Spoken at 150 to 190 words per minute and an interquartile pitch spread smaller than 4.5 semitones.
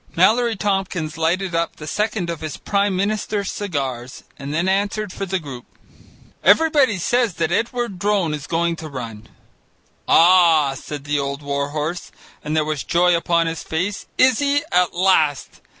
No: average, 165 wpm; average, 4.9 semitones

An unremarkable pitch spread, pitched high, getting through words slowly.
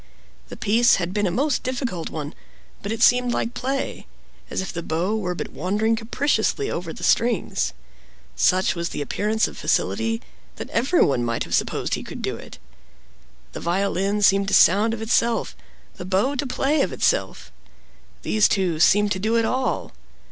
No: average, 4.7 semitones; high, 210 Hz; average, 170 wpm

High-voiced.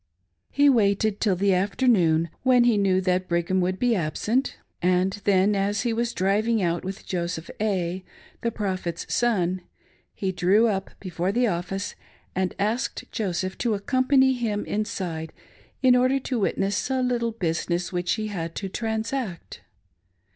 Yes: high, 200 Hz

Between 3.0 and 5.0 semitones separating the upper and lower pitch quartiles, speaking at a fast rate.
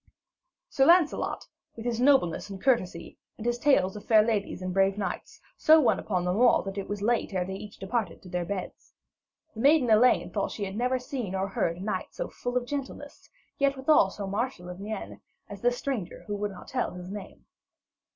Yes: average, 4.6 semitones; fast, 215 wpm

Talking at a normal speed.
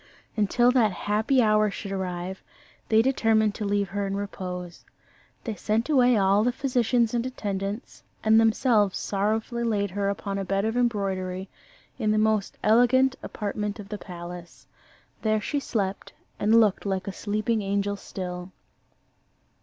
Yes: average, 150 wpm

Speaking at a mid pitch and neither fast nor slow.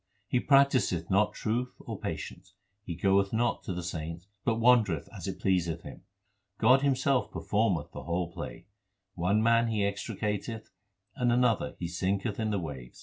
No: low, 100 Hz; average, 165 wpm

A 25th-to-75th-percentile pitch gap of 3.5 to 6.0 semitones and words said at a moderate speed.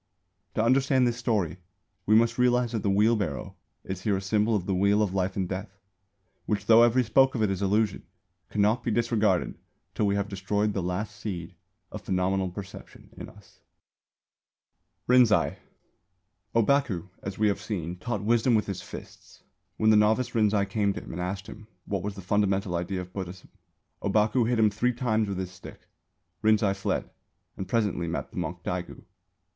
No: average, 2.8 semitones; average, 180 wpm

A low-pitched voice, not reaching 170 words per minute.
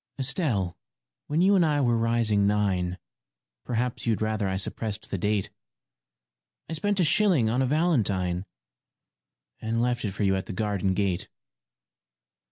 Yes: low, 110 Hz; average, 155 wpm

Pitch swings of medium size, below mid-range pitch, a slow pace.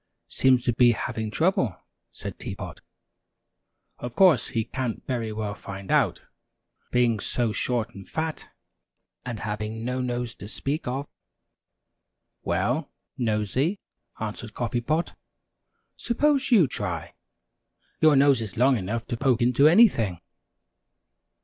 Yes: average, 4.0 semitones; low, 120 Hz; slow, 125 wpm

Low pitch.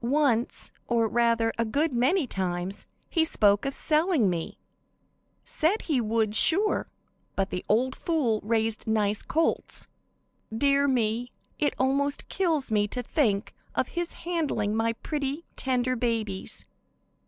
No: high, 240 Hz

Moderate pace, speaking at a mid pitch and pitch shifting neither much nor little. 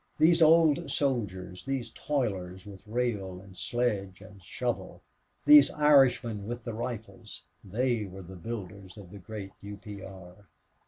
No: average, 145 wpm; low, 105 Hz; average, 4.5 semitones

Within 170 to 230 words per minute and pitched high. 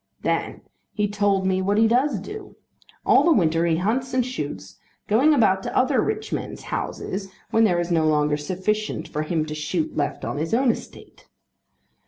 Yes: average, 185 wpm; high, 195 Hz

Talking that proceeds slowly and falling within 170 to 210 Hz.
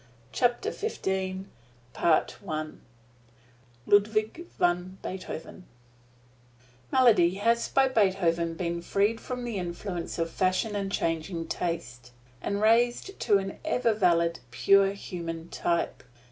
Yes: slow, 105 wpm; high, 190 Hz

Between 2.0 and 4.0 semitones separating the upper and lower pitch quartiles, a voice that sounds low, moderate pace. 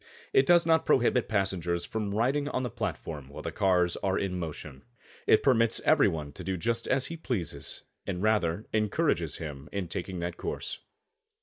No: wide, 5.5 semitones; very low, 95 Hz; average, 180 wpm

